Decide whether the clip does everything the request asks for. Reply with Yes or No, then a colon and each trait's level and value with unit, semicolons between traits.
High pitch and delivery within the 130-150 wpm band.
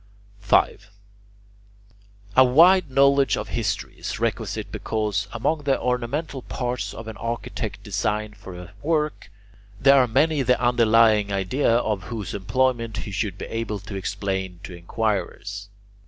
No: low, 115 Hz; average, 140 wpm